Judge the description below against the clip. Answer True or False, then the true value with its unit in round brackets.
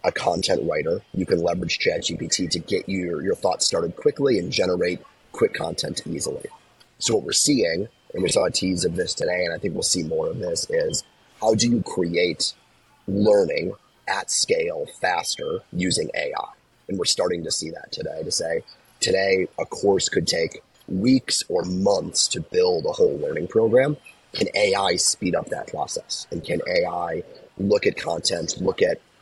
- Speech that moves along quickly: False (180 wpm)